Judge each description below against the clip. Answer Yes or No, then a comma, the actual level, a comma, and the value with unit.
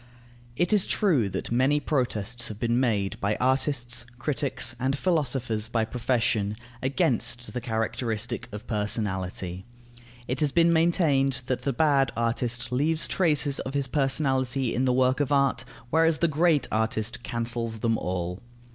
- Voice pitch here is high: No, low, 125 Hz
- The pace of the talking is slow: No, average, 145 wpm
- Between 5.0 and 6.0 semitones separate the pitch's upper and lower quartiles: No, average, 3.6 semitones